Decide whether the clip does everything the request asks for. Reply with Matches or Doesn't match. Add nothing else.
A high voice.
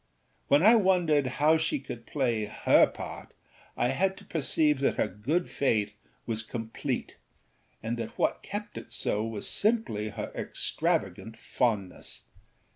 Doesn't match